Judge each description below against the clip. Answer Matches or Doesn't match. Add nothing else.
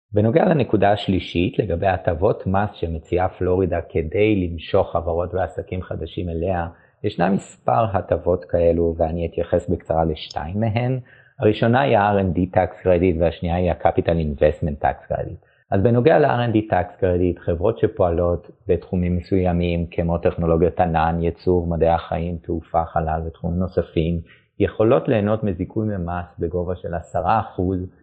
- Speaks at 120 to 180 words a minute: Matches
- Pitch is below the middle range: Matches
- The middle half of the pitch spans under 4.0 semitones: Matches